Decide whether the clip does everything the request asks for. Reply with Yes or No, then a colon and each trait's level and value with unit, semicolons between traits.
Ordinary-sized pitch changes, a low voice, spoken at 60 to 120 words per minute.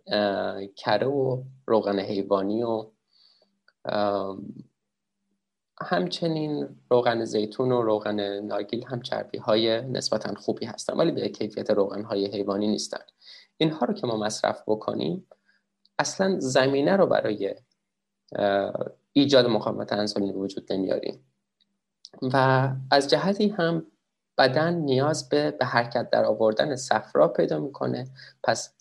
No: wide, 6.3 semitones; low, 120 Hz; average, 110 wpm